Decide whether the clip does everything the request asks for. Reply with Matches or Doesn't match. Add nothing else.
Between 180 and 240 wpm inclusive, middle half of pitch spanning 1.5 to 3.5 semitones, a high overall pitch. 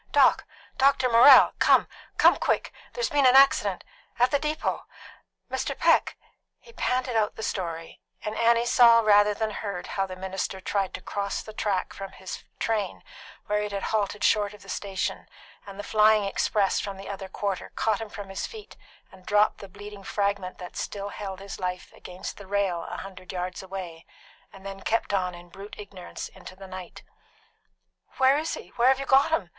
Matches